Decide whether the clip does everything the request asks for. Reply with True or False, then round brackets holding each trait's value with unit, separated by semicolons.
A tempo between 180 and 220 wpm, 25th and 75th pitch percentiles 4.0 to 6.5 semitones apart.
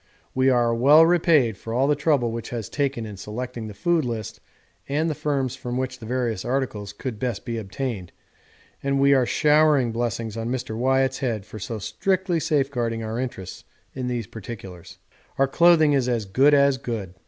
False (185 wpm; 3.6 semitones)